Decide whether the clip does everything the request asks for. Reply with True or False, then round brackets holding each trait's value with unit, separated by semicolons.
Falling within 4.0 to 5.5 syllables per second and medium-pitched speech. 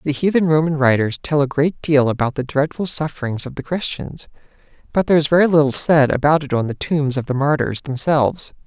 False (5.8 syllables/s; 145 Hz)